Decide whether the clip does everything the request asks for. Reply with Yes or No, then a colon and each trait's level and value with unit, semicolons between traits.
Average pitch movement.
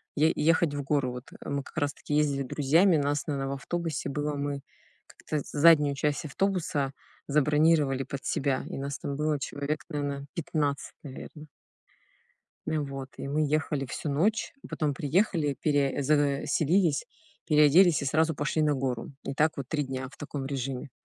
No: narrow, 1.8 semitones